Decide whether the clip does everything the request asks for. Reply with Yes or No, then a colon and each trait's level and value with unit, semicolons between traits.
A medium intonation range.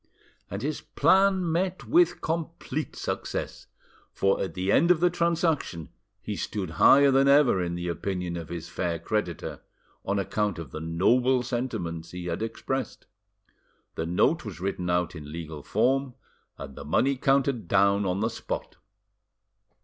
No: wide, 8.2 semitones